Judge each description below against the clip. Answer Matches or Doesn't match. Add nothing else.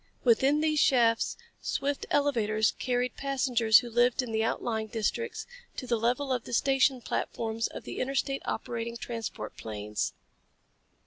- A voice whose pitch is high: Matches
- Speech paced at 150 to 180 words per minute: Doesn't match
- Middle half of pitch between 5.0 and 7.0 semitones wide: Doesn't match